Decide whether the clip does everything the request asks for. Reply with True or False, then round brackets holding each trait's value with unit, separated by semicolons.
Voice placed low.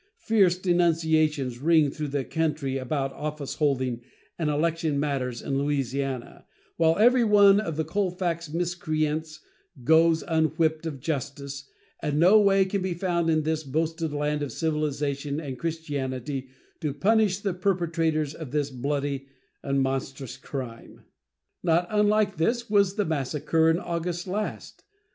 False (155 Hz)